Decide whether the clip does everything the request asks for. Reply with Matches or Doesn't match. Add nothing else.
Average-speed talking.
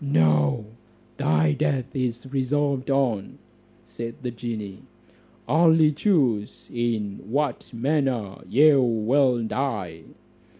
Doesn't match